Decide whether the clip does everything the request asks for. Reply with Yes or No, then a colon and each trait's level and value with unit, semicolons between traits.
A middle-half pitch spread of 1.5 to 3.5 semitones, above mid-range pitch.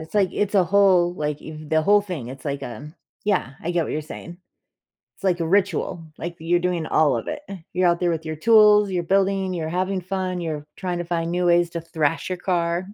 No: average, 2.8 semitones; medium, 175 Hz